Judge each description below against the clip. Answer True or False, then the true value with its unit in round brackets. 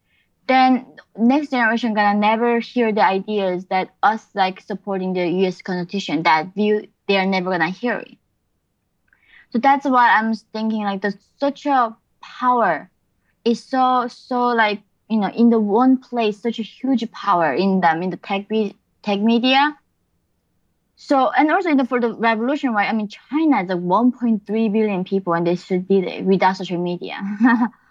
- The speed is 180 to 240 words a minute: False (170 wpm)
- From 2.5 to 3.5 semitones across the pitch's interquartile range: False (4.3 semitones)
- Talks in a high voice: True (220 Hz)